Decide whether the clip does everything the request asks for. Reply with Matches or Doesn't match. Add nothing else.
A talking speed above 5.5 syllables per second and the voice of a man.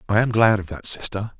Matches